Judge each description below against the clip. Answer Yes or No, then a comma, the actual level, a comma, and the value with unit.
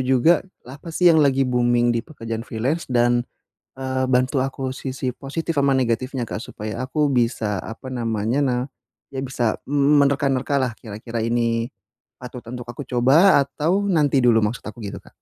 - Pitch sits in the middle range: No, low, 130 Hz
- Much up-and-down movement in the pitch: No, average, 2.8 semitones